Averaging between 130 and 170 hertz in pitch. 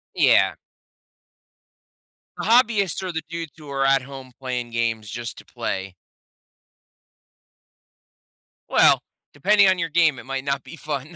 Yes: medium, 140 Hz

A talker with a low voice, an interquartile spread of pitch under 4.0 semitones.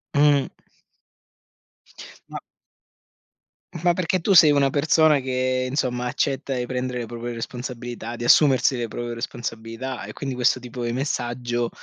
Yes: low, 125 Hz; narrow, 2.5 semitones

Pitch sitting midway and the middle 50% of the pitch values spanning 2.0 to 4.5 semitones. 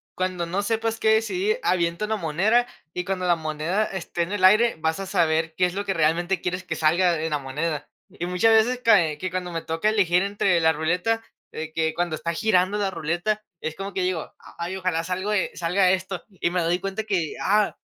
Yes: medium, 180 Hz; average, 3.3 semitones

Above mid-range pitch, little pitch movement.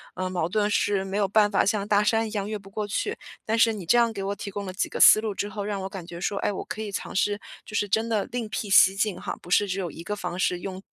Yes: high, 205 Hz; narrow, 1.8 semitones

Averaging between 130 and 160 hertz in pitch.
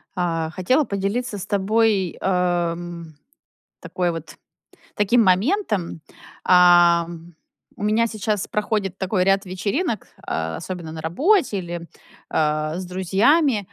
No: medium, 185 Hz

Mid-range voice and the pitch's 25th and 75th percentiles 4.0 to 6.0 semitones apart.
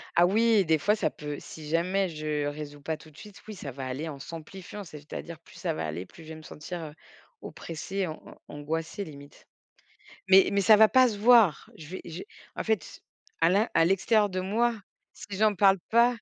Yes: medium, 170 Hz; average, 5.0 semitones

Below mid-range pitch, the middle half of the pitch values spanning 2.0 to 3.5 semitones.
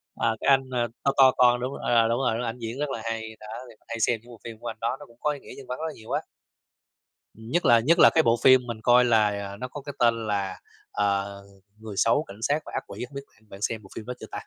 Yes: low, 115 Hz; average, 2.8 semitones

